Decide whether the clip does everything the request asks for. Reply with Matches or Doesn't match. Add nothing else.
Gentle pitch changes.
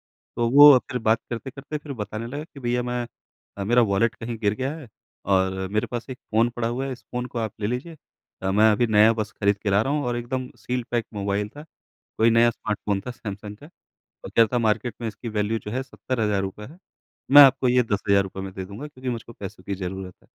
Doesn't match